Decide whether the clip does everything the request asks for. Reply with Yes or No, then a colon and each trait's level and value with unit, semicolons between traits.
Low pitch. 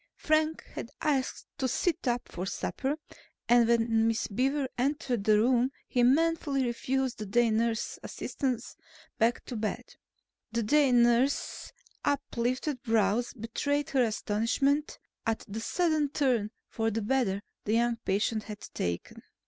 No: high, 240 Hz